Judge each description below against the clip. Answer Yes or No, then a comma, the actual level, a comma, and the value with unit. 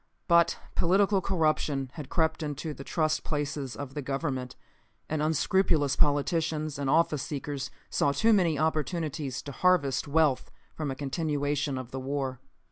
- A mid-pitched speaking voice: Yes, medium, 150 Hz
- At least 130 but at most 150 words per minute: Yes, average, 145 wpm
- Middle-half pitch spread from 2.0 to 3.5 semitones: Yes, average, 2.8 semitones